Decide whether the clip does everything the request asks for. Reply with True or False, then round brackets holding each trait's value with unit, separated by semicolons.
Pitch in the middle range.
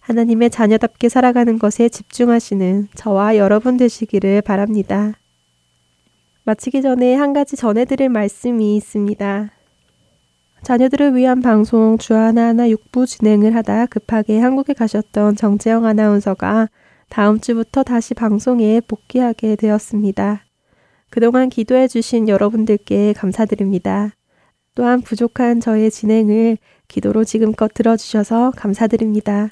False (220 Hz)